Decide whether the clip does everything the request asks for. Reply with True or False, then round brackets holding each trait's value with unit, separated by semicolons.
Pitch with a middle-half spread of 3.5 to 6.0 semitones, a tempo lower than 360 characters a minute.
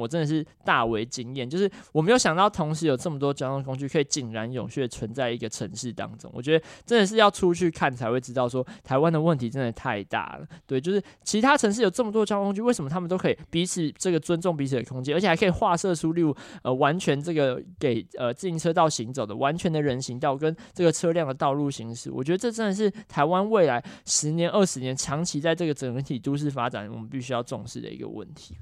False (5.6 semitones; 375 characters per minute)